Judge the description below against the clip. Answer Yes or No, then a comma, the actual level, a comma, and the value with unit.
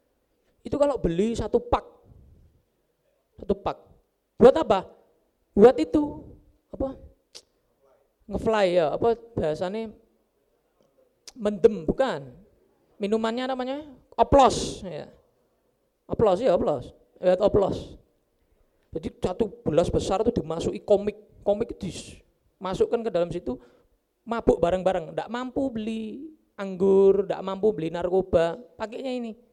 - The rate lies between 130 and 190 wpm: No, average, 100 wpm